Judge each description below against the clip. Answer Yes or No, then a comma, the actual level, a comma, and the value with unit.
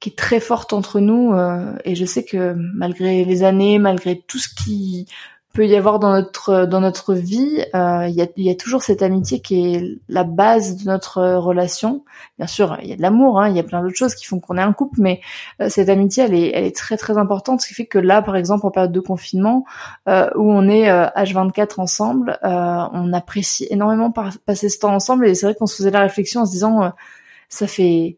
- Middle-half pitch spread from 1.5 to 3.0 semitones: Yes, narrow, 2.6 semitones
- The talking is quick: Yes, fast, 245 wpm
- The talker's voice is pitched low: No, high, 195 Hz